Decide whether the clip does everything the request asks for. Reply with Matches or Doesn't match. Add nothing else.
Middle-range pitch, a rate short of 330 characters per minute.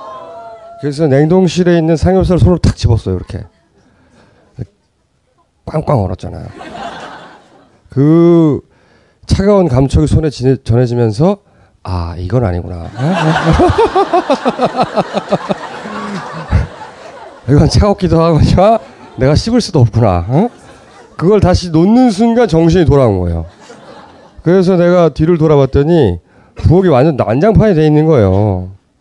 Matches